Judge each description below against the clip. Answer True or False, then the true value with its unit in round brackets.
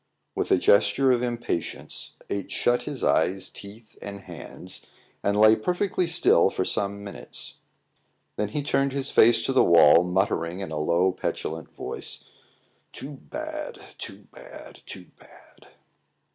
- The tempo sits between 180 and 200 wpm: False (145 wpm)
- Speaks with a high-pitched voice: False (105 Hz)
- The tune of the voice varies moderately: False (6.4 semitones)